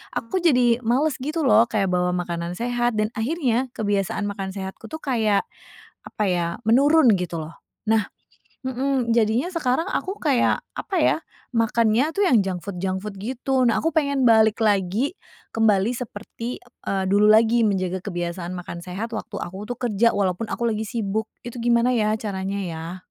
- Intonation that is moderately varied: Yes, average, 4.2 semitones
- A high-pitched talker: Yes, high, 220 Hz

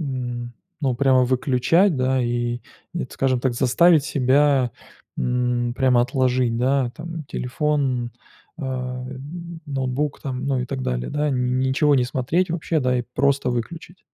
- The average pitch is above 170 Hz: No, low, 130 Hz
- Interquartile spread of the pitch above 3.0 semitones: No, narrow, 2.4 semitones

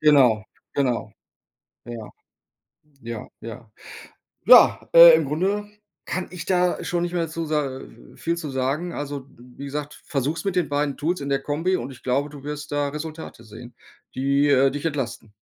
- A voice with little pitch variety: No, average, 3.6 semitones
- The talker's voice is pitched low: No, medium, 145 Hz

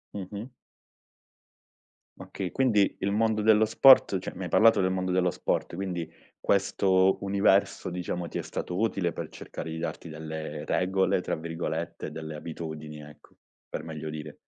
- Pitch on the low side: Yes, very low, 90 Hz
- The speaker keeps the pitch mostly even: No, average, 3.8 semitones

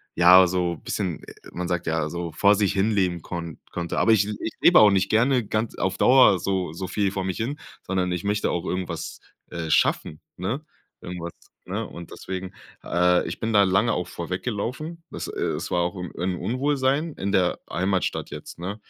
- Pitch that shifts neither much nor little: Yes, average, 3.4 semitones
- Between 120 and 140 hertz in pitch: No, very low, 95 Hz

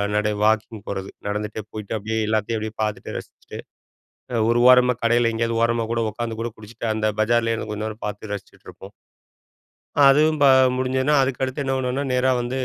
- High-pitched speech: No, low, 115 Hz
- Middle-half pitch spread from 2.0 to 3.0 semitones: Yes, average, 2.7 semitones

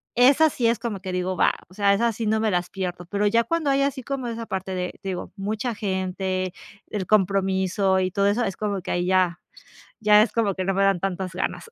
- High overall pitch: Yes, high, 195 Hz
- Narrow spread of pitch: No, average, 3.2 semitones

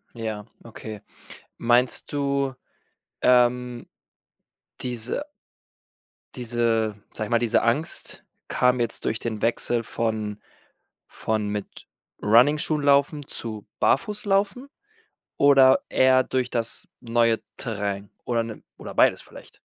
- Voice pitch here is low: Yes, low, 120 Hz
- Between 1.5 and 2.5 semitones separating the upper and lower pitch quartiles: No, average, 2.9 semitones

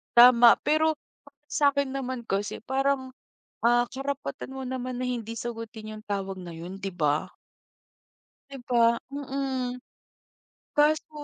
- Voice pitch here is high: Yes, very high, 255 Hz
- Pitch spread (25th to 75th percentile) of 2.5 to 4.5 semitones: Yes, average, 3.5 semitones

